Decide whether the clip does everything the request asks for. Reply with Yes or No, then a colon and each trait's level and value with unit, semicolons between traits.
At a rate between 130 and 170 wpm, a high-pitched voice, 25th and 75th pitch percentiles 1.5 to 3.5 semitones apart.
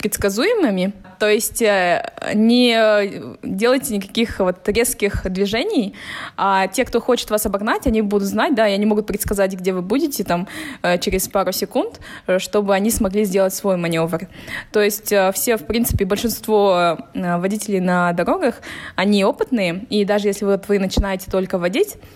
Yes: average, 150 wpm; high, 205 Hz; average, 2.9 semitones